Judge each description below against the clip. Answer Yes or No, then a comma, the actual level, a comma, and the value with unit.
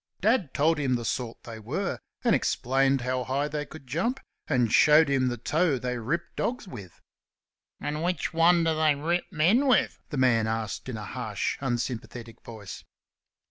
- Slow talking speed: No, average, 175 wpm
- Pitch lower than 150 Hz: Yes, low, 135 Hz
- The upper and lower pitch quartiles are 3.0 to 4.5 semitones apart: No, average, 5.1 semitones